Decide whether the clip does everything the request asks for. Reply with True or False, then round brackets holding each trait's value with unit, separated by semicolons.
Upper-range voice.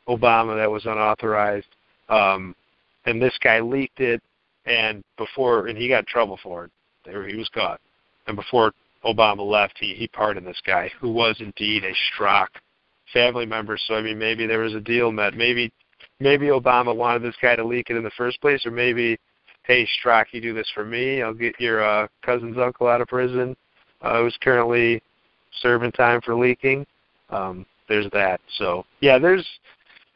False (115 Hz)